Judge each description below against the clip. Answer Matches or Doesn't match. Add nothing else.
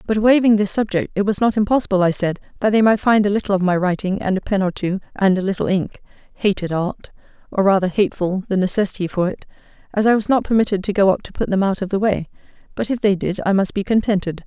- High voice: Matches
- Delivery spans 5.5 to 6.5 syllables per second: Matches